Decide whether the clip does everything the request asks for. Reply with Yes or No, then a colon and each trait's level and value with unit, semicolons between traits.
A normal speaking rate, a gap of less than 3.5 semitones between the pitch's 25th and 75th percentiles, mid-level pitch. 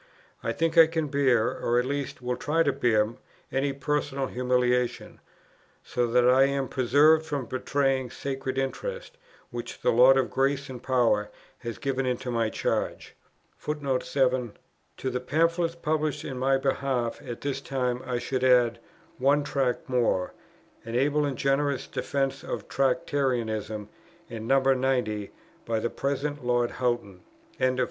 No: average, 150 wpm; narrow, 2.4 semitones; low, 130 Hz